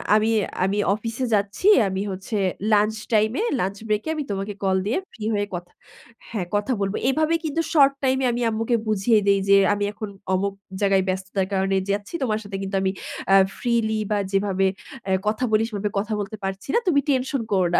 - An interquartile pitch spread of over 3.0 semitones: No, average, 2.7 semitones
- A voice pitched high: Yes, high, 205 Hz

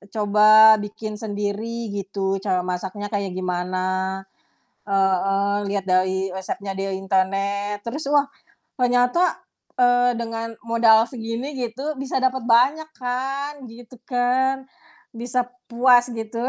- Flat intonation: No, average, 4.0 semitones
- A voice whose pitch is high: Yes, high, 220 Hz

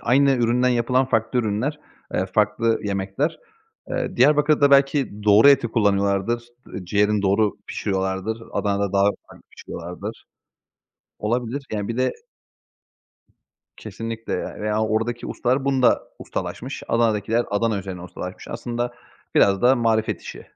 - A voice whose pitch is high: No, low, 115 Hz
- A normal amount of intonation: Yes, average, 3.3 semitones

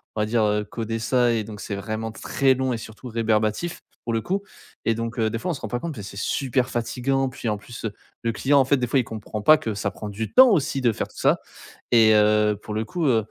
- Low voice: Yes, low, 115 Hz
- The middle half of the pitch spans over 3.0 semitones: Yes, average, 3.4 semitones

